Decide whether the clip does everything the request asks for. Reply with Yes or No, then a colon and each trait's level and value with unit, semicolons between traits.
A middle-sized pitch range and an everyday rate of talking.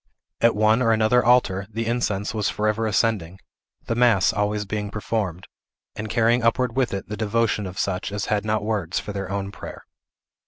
No: narrow, 2.2 semitones; average, 185 wpm